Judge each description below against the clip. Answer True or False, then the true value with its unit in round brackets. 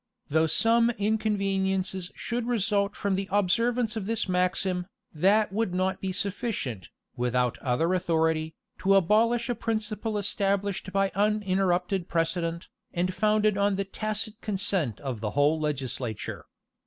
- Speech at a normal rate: False (130 wpm)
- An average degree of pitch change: True (3.9 semitones)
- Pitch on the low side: False (195 Hz)